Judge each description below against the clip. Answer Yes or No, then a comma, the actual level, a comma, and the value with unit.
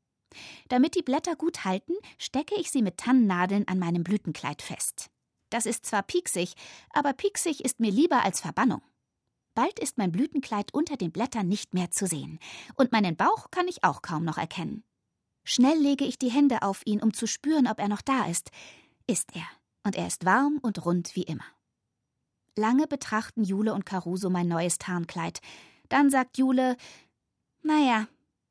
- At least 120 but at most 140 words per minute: No, average, 175 wpm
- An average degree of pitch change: No, wide, 7.5 semitones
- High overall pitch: Yes, high, 220 Hz